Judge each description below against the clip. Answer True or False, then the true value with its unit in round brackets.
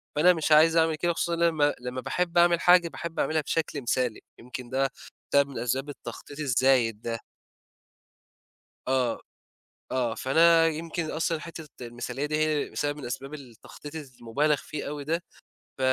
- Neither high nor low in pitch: True (145 Hz)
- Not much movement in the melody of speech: False (4.0 semitones)